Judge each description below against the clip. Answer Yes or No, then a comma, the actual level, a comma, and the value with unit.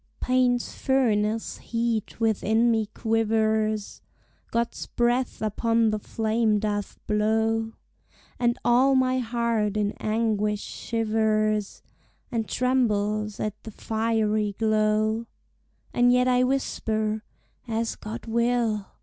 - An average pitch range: No, narrow, 1.7 semitones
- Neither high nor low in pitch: No, high, 225 Hz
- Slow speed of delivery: Yes, slow, 105 wpm